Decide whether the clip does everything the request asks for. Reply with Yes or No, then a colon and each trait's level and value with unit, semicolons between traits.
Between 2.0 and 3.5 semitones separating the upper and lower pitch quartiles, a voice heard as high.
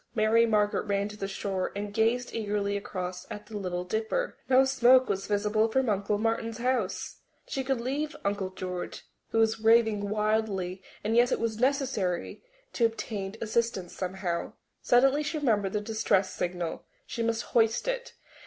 Yes: average, 2.9 semitones; high, 215 Hz